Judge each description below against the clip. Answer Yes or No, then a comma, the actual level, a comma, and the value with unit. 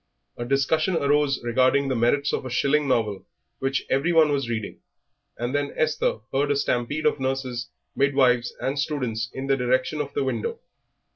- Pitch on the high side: No, low, 135 Hz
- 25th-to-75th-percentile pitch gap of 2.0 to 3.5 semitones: Yes, average, 2.7 semitones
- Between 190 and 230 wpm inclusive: No, average, 170 wpm